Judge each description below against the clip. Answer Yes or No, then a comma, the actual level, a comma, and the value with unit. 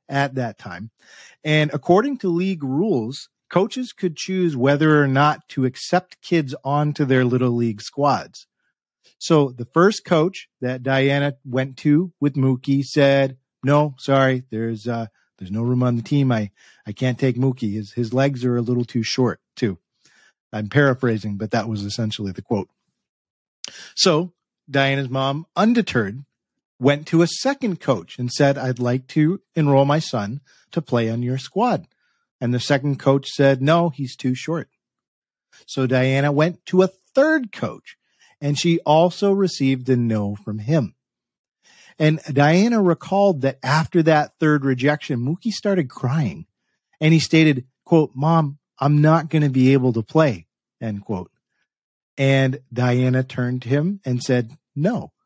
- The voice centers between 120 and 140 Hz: Yes, low, 135 Hz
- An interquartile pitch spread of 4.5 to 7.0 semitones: No, average, 4.0 semitones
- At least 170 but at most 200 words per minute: No, average, 155 wpm